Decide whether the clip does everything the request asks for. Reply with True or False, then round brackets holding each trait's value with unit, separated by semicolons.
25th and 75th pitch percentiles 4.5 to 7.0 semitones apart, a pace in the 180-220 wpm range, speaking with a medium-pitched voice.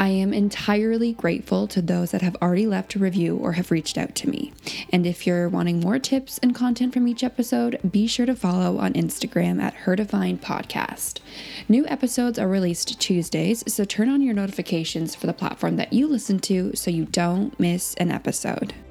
False (5.2 semitones; 190 wpm; 195 Hz)